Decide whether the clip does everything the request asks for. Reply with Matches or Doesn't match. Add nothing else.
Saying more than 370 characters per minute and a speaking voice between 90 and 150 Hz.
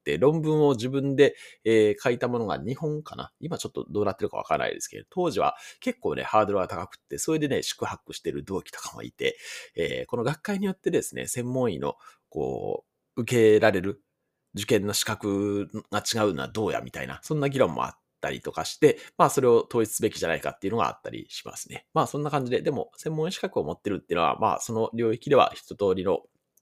Matches